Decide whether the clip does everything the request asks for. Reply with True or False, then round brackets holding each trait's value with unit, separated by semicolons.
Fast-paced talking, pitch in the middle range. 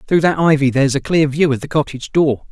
True (260 wpm; 145 Hz)